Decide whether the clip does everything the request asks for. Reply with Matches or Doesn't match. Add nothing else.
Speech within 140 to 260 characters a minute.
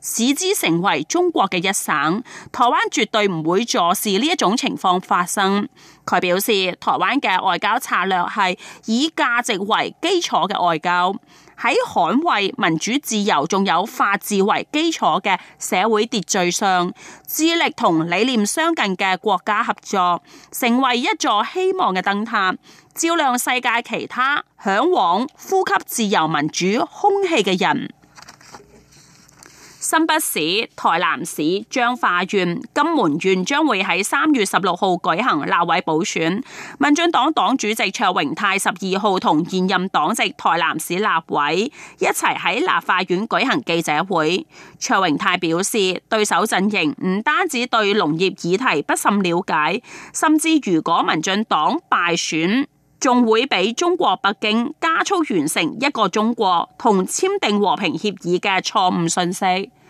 Matches